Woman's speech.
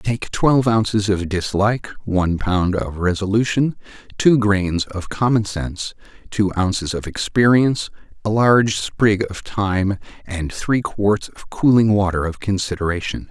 No: male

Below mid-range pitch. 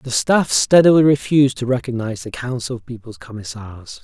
Yes: low, 125 Hz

